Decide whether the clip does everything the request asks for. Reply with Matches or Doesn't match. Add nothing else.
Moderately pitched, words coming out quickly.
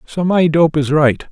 Matches